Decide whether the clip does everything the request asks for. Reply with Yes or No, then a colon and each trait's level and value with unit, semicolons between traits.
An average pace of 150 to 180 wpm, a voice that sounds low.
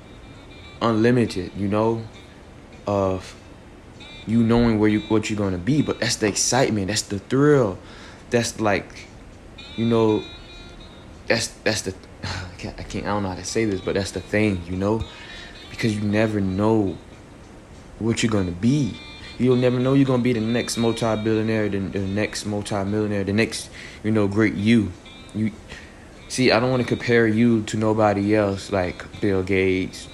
Yes: average, 175 wpm; low, 105 Hz